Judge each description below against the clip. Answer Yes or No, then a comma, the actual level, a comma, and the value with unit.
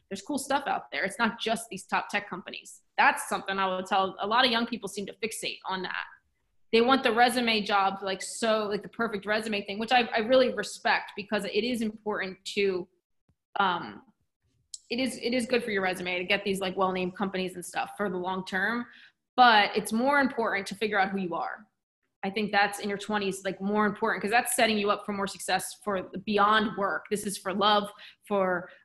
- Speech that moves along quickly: Yes, fast, 220 wpm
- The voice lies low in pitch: No, high, 205 Hz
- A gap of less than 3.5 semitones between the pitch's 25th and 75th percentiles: Yes, average, 2.8 semitones